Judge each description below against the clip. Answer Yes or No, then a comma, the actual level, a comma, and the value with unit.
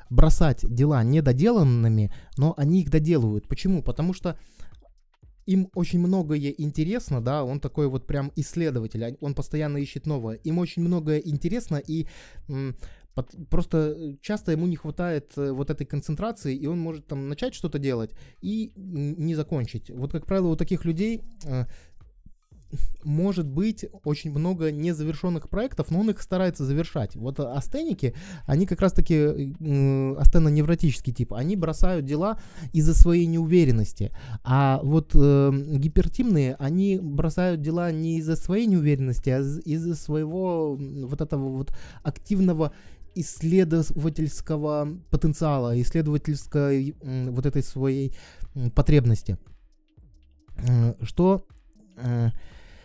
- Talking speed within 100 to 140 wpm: Yes, average, 125 wpm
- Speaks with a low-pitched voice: No, medium, 150 Hz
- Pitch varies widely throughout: No, average, 3.9 semitones